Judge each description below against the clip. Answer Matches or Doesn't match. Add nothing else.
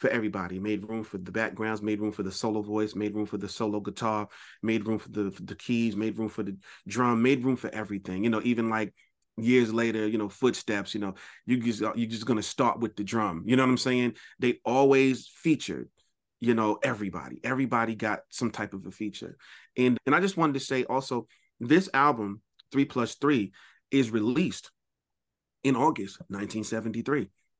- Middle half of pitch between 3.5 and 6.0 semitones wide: Doesn't match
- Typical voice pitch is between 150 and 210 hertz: Doesn't match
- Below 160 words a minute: Doesn't match